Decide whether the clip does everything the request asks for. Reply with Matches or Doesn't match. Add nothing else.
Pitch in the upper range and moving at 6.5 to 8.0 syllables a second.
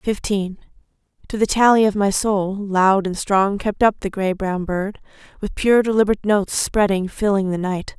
Doesn't match